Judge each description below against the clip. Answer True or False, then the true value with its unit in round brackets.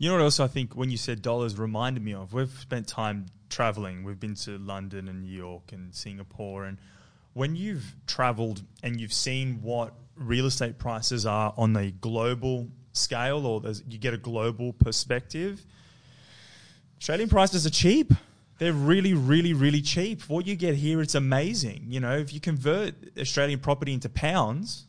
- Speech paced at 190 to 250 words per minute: False (175 wpm)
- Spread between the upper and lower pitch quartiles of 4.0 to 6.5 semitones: True (4.6 semitones)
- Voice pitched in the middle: False (125 Hz)